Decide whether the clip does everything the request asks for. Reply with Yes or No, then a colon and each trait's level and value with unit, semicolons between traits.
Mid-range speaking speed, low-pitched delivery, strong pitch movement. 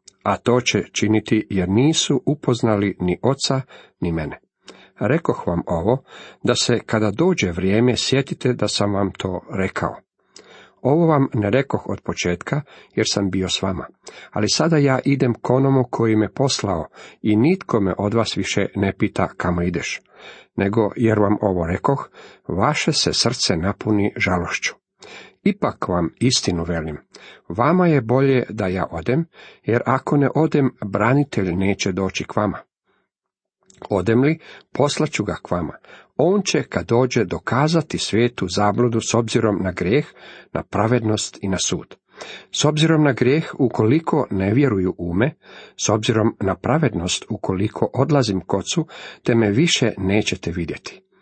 Yes: average, 150 wpm; low, 110 Hz; wide, 5.7 semitones